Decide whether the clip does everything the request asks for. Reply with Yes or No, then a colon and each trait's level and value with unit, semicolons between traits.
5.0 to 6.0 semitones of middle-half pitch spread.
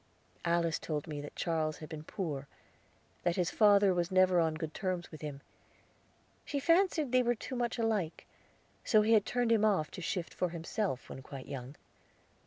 Yes: wide, 5.6 semitones